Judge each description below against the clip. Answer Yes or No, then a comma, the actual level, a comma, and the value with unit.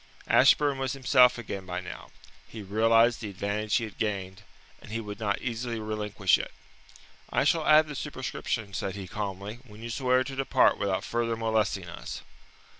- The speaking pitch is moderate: No, low, 110 Hz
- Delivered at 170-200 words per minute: Yes, average, 175 wpm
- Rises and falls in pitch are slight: No, average, 3.8 semitones